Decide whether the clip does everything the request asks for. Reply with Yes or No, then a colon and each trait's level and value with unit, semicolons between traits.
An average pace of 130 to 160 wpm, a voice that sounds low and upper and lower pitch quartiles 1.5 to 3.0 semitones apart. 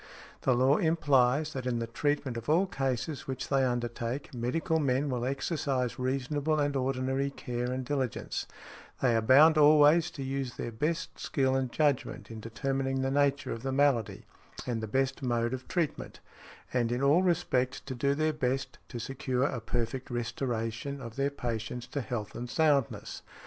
No: average, 170 wpm; low, 130 Hz; average, 2.7 semitones